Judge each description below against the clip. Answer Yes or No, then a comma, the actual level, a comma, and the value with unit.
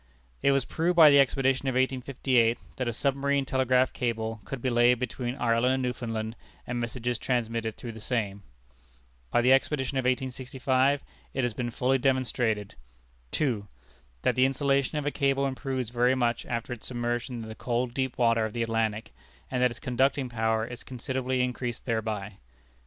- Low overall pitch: Yes, low, 125 Hz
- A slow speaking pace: No, average, 175 wpm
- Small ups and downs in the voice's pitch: Yes, narrow, 2.2 semitones